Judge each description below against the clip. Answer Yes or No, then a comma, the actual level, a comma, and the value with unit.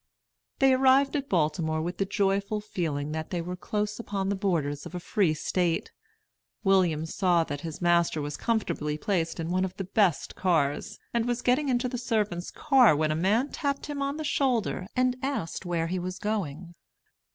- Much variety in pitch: Yes, wide, 6.0 semitones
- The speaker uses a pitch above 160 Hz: Yes, high, 190 Hz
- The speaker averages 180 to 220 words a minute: Yes, average, 185 wpm